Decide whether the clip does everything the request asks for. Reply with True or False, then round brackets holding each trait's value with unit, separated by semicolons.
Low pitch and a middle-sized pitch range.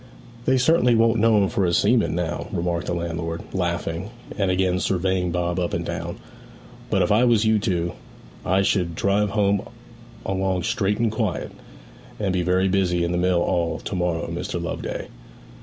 True (95 Hz; 3.1 semitones)